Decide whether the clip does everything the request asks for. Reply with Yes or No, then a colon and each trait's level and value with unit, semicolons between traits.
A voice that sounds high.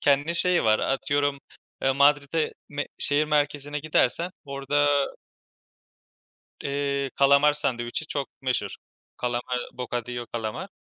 No: medium, 140 Hz